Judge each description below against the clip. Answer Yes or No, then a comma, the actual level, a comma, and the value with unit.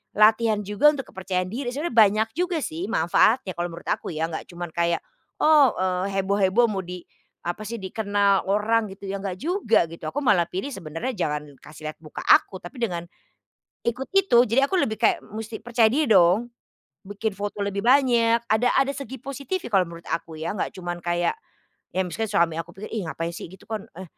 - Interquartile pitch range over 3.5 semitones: Yes, average, 5.1 semitones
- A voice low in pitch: No, high, 205 Hz